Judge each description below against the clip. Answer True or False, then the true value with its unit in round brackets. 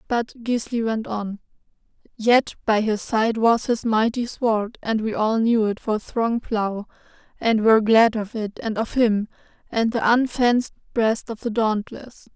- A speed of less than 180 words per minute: True (170 wpm)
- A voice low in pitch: False (225 Hz)